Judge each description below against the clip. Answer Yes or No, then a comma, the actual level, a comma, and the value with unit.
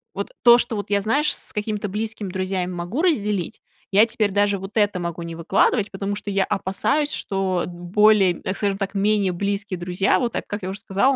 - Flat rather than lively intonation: Yes, narrow, 2.2 semitones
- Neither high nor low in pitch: No, high, 200 Hz